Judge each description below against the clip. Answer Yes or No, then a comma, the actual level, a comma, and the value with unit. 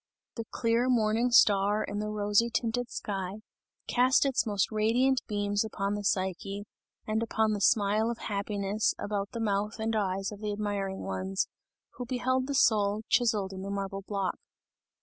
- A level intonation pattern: Yes, narrow, 2.3 semitones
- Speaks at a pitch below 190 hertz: No, high, 210 Hz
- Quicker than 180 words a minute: No, average, 165 wpm